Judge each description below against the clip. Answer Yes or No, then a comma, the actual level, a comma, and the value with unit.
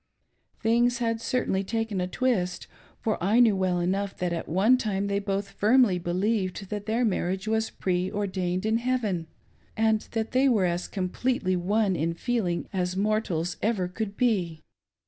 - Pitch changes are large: No, average, 3.6 semitones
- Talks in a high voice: Yes, high, 200 Hz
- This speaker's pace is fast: No, average, 160 wpm